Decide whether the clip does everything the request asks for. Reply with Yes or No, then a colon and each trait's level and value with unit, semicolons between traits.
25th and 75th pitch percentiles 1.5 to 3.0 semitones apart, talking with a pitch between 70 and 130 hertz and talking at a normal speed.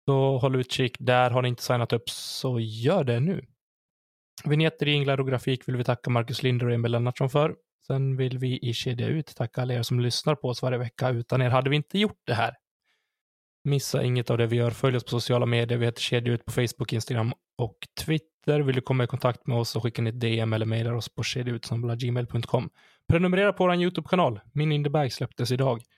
No: average, 2.7 semitones; low, 125 Hz; fast, 215 wpm